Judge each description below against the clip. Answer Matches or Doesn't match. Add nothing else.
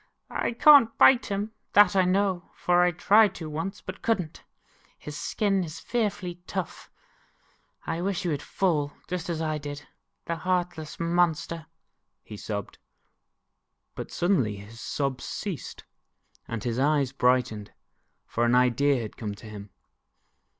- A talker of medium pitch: Matches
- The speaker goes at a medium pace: Matches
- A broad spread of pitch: Matches